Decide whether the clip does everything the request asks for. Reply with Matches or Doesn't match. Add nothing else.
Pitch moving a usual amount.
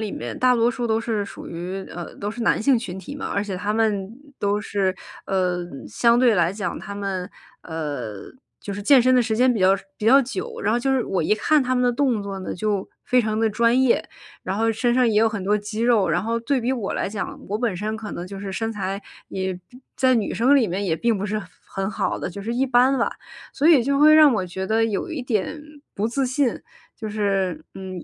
Matches